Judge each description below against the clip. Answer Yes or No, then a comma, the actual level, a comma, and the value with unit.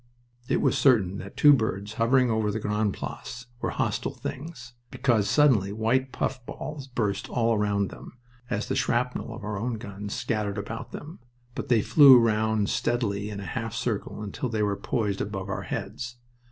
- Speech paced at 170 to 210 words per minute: Yes, average, 175 wpm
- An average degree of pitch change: Yes, average, 3.3 semitones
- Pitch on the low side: Yes, low, 110 Hz